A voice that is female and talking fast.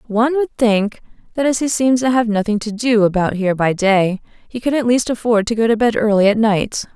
Yes: female; fast, 240 wpm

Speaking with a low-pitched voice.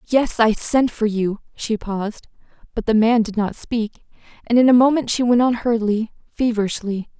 No: high, 225 Hz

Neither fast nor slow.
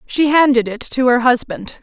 Yes: average, 195 wpm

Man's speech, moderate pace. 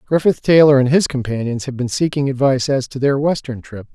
No: male; fast, 215 wpm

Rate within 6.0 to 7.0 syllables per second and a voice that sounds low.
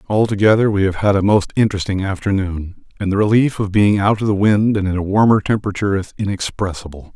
Yes: 6.3 syllables/s; low, 100 Hz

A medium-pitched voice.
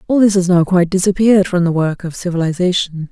Yes: medium, 180 Hz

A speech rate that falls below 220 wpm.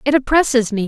Yes: fast, 205 wpm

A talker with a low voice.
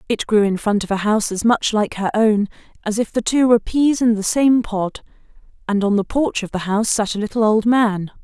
No: high, 215 Hz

